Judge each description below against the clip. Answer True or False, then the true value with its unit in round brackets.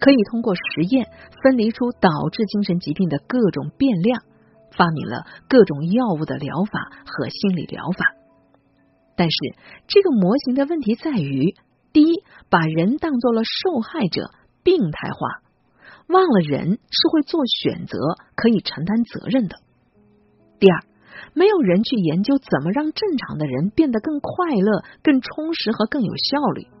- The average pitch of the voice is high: True (215 Hz)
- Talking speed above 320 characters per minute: False (230 characters per minute)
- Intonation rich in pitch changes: True (8.4 semitones)